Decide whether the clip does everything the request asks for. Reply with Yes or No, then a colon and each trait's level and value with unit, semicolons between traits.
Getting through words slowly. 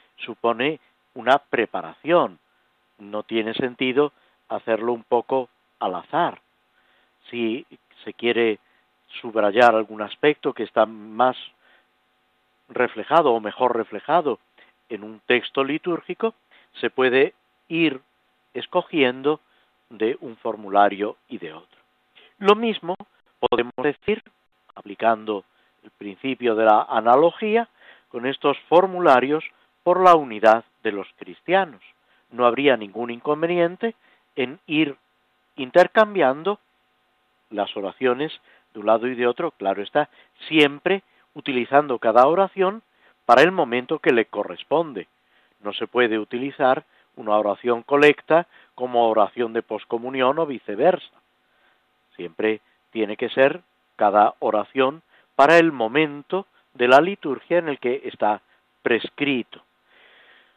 Yes: slow, 115 wpm